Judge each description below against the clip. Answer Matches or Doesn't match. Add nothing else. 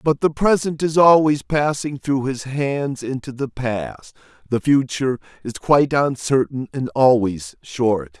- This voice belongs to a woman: Doesn't match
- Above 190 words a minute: Doesn't match